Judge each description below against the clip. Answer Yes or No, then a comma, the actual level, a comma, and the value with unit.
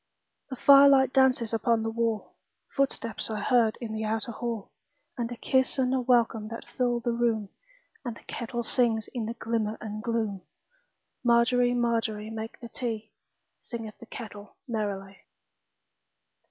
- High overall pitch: Yes, high, 230 Hz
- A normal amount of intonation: No, narrow, 2.0 semitones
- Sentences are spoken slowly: Yes, slow, 130 wpm